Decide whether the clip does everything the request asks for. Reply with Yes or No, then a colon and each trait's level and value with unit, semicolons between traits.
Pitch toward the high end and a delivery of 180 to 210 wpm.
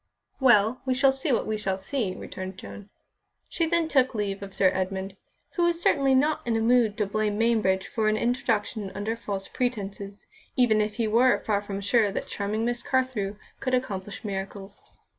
Yes: high, 215 Hz; average, 185 wpm